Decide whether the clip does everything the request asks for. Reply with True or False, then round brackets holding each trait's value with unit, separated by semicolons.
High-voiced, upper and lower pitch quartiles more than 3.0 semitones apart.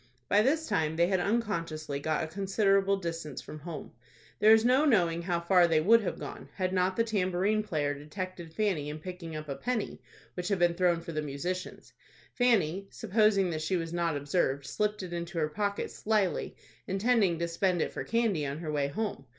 False (180 Hz; 4.2 semitones)